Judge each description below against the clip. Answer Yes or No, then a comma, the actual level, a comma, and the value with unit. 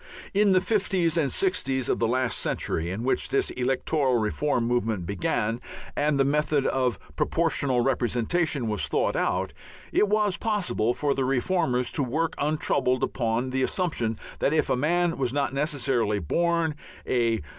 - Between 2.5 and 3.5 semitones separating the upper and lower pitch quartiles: No, average, 5.1 semitones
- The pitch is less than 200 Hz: Yes, low, 135 Hz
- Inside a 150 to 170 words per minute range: Yes, average, 155 wpm